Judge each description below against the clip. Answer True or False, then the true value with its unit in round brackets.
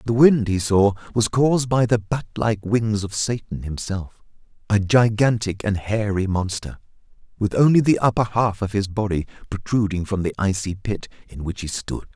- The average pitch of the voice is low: True (105 Hz)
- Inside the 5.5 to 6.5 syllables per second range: False (4.9 syllables/s)